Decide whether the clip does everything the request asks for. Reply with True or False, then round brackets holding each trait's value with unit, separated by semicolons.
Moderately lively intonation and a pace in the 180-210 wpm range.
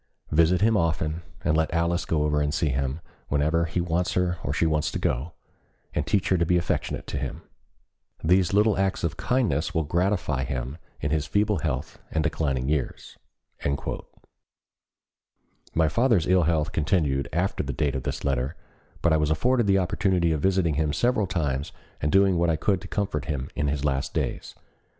True (3.6 semitones; 185 wpm)